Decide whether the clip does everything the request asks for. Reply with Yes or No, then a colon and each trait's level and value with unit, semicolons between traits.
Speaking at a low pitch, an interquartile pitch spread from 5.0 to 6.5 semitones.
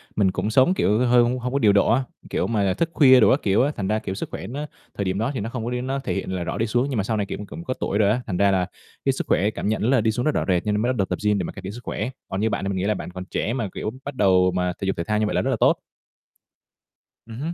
No: low, 110 Hz; average, 4.3 semitones